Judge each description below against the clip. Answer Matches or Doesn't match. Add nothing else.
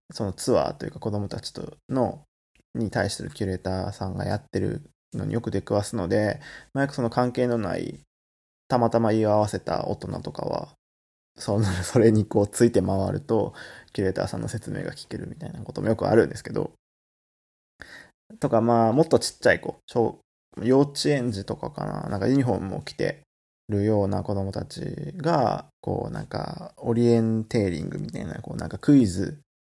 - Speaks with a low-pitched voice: Matches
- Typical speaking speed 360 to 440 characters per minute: Matches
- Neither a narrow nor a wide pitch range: Matches